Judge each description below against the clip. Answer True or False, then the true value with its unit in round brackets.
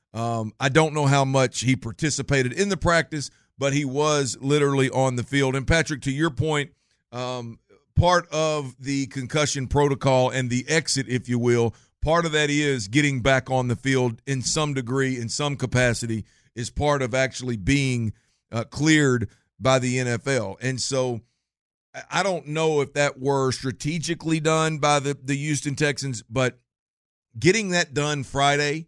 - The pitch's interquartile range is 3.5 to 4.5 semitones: False (2.9 semitones)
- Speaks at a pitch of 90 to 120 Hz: False (135 Hz)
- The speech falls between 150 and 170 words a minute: True (165 wpm)